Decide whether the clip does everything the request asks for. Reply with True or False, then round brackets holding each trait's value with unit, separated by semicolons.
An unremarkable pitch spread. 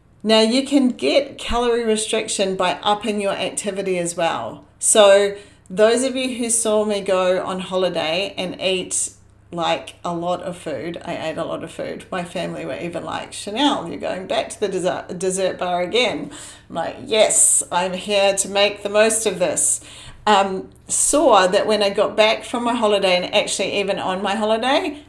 True (3.0 semitones)